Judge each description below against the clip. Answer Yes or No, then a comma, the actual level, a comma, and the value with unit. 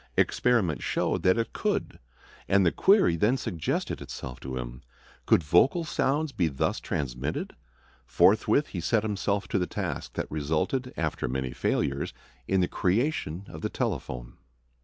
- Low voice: Yes, very low, 90 Hz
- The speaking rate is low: No, average, 150 wpm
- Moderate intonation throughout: No, wide, 8.2 semitones